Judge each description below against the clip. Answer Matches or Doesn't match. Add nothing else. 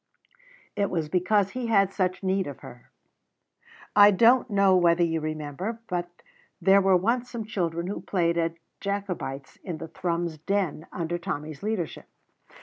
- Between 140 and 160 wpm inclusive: Matches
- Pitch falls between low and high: Matches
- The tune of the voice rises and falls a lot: Doesn't match